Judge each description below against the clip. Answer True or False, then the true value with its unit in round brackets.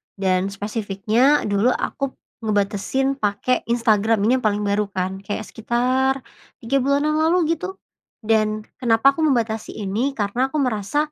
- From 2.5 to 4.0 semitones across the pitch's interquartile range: False (4.6 semitones)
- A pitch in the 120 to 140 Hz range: False (225 Hz)